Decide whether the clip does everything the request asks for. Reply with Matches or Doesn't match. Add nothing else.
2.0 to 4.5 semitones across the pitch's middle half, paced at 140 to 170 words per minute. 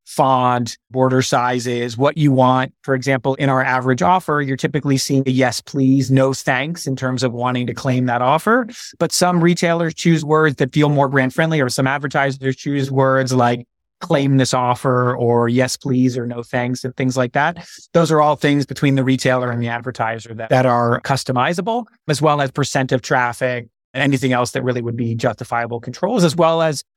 Doesn't match